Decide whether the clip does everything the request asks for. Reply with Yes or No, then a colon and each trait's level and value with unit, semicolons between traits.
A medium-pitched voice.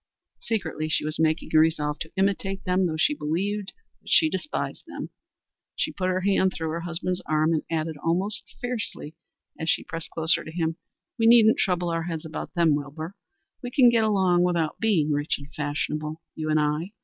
Yes: medium, 165 Hz